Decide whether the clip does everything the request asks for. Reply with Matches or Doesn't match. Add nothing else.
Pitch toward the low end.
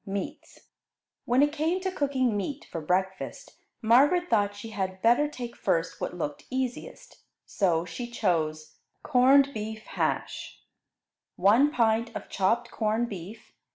Doesn't match